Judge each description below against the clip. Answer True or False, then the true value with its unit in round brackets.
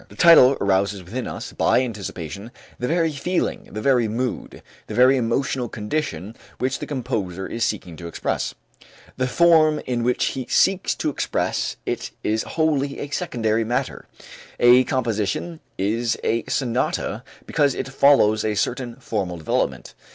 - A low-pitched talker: True (120 Hz)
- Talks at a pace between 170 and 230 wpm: False (150 wpm)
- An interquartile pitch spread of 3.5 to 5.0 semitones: True (4.4 semitones)